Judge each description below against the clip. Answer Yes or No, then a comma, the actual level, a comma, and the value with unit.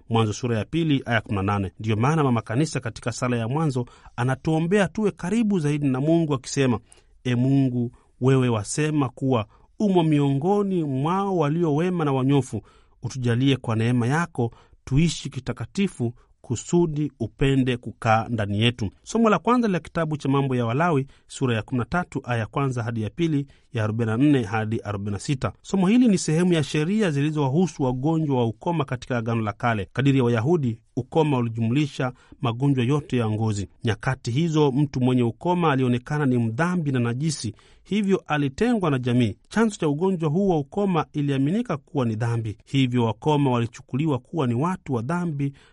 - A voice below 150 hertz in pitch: Yes, low, 135 Hz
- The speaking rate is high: Yes, fast, 150 wpm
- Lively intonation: No, average, 5.0 semitones